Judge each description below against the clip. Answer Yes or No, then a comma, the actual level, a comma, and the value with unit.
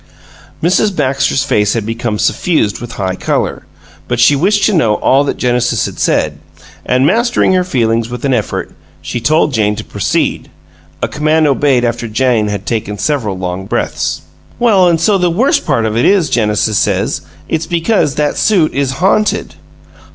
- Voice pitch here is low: Yes, low, 130 Hz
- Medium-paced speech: Yes, average, 175 wpm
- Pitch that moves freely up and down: Yes, wide, 6.7 semitones